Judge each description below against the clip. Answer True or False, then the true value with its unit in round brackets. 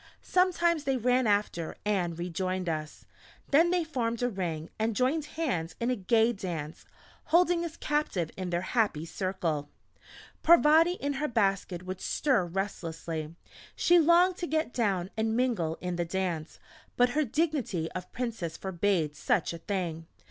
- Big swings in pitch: True (8.6 semitones)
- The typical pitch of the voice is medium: False (205 Hz)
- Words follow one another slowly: False (155 wpm)